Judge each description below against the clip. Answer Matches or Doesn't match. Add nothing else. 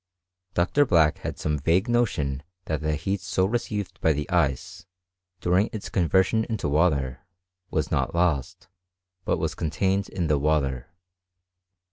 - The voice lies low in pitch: Matches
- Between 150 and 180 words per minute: Doesn't match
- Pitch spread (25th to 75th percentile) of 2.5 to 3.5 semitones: Doesn't match